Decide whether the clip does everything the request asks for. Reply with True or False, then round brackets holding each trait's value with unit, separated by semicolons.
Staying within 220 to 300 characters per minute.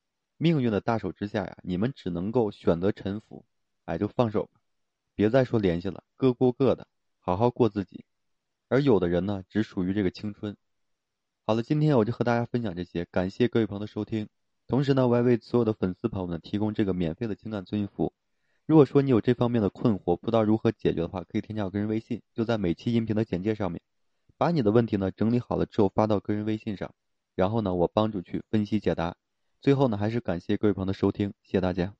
False (350 characters per minute)